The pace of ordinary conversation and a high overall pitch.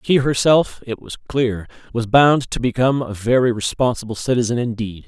No: average, 165 wpm; low, 120 Hz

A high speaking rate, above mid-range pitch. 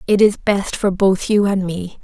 Yes: fast, 235 wpm; high, 195 Hz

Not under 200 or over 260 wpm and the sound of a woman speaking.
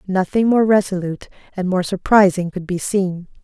No: average, 155 wpm; female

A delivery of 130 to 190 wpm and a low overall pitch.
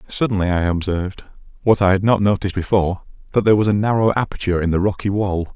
No: fast, 205 wpm; low, 100 Hz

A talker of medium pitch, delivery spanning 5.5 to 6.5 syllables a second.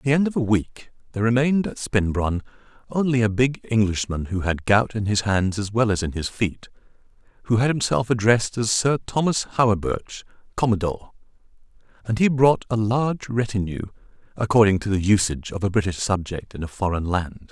No: low, 110 Hz; 5.6 syllables/s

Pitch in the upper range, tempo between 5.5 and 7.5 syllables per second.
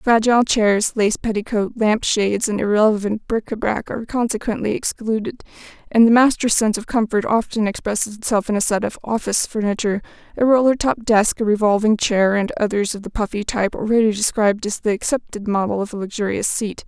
Yes: high, 215 Hz; 5.9 syllables/s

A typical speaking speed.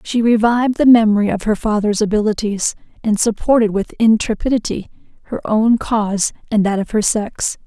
Yes: average, 155 wpm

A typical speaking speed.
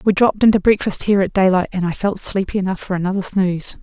No: fast, 250 wpm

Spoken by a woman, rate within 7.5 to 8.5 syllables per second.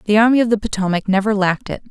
Yes: female; 7.7 syllables/s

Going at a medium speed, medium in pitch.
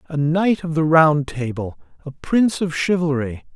Yes: average, 170 wpm; medium, 155 Hz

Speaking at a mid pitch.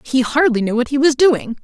No: very high, 265 Hz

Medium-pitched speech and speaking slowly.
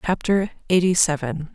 Yes: medium, 170 Hz; slow, 115 wpm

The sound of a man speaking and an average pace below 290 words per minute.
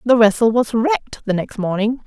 No: female; fast, 205 wpm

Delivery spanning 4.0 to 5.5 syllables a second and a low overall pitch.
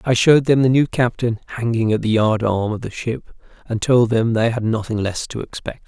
Yes: 5.3 syllables/s; low, 115 Hz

